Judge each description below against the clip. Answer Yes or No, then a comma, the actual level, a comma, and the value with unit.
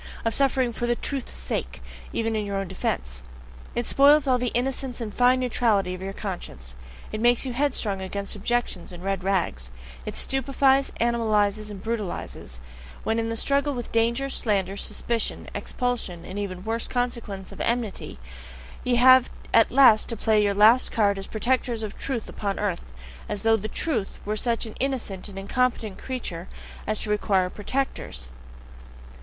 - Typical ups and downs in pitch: Yes, average, 3.9 semitones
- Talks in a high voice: Yes, high, 225 Hz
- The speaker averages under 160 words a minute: No, average, 165 wpm